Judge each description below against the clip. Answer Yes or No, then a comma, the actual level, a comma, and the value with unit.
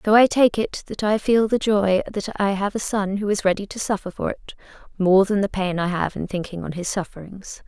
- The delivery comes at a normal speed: No, fast, 250 wpm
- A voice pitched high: Yes, high, 200 Hz